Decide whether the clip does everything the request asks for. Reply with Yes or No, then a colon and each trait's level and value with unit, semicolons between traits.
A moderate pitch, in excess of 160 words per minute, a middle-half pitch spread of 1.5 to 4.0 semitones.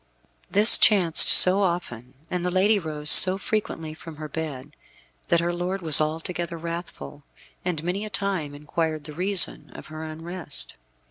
No: medium, 170 Hz; average, 155 wpm; average, 3.0 semitones